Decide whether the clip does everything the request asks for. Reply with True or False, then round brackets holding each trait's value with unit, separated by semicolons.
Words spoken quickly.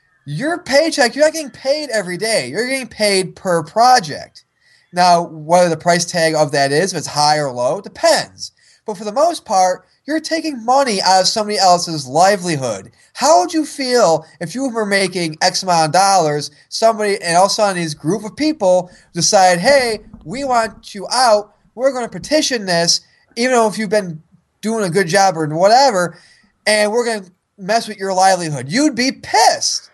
False (190 wpm)